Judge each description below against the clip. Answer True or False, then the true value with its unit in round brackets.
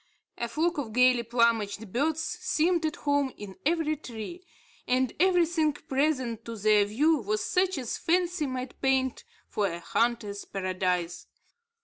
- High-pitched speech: True (255 Hz)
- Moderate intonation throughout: False (6.4 semitones)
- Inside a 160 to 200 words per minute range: False (140 wpm)